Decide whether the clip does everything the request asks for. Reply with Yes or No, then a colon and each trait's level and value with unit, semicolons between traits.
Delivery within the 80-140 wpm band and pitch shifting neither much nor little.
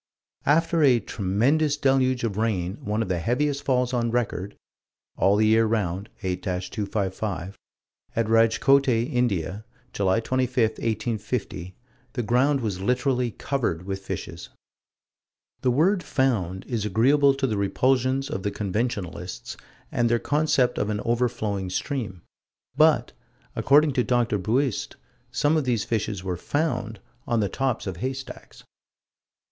Yes: slow, 135 wpm; average, 4.6 semitones